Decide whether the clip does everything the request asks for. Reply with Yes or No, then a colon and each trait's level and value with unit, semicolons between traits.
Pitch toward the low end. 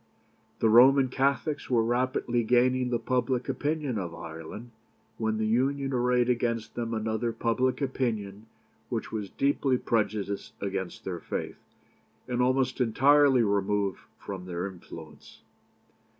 Yes: low, 120 Hz